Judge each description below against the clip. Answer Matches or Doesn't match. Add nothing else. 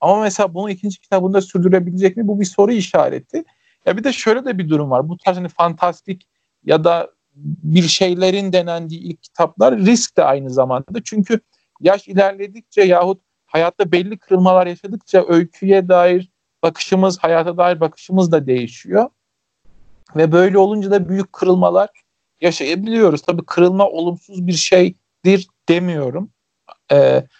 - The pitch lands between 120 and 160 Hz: Doesn't match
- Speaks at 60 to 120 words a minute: Doesn't match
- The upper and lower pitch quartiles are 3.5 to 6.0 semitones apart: Doesn't match